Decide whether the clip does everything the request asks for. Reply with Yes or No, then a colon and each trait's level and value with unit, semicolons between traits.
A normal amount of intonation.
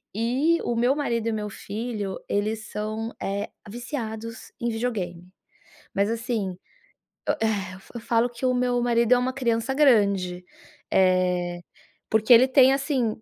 Yes: average, 3.2 semitones